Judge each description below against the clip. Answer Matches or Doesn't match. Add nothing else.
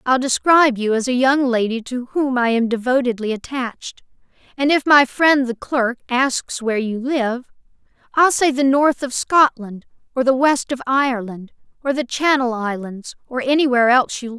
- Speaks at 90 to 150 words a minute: Doesn't match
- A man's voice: Doesn't match